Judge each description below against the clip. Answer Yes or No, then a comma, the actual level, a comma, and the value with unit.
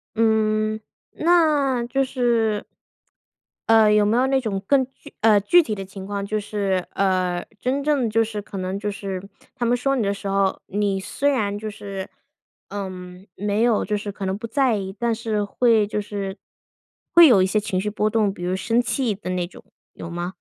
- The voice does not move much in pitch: No, average, 3.0 semitones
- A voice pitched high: Yes, high, 210 Hz